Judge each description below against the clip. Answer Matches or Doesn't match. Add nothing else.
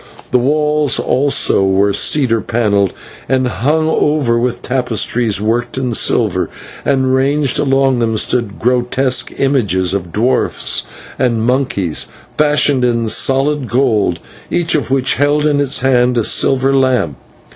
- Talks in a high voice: Doesn't match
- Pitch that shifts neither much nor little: Matches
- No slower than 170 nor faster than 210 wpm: Doesn't match